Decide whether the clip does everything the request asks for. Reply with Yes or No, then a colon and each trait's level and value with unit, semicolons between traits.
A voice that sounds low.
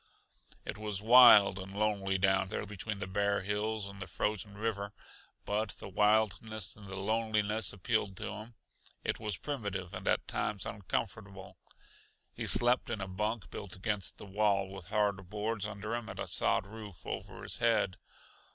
Yes: low, 105 Hz